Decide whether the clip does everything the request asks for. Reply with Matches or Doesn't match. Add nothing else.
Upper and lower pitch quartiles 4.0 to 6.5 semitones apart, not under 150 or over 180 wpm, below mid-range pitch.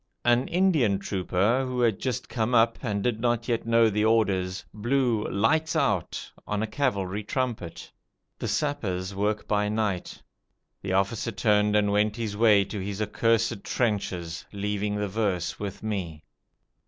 Doesn't match